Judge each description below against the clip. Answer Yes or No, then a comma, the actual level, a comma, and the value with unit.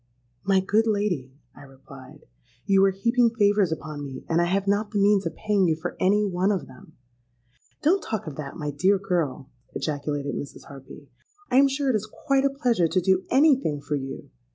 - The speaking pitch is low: No, medium, 185 Hz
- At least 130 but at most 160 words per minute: No, average, 195 wpm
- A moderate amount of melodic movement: No, wide, 6.5 semitones